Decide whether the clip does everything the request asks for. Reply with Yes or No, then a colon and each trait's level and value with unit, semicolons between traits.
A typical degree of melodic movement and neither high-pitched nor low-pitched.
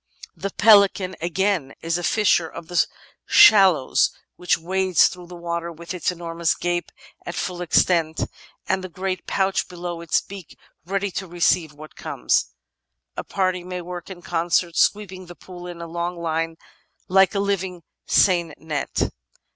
No: narrow, 1.9 semitones; medium, 175 Hz